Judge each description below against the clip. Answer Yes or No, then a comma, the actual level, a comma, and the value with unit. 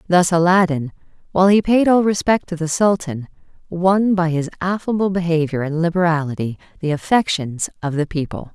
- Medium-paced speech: Yes, average, 155 wpm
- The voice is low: No, medium, 170 Hz